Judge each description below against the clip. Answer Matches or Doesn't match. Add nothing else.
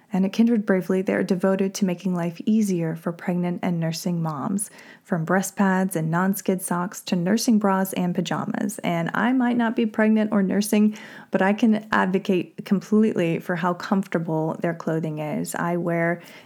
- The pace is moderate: Matches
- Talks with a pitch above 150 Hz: Matches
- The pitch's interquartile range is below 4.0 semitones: Matches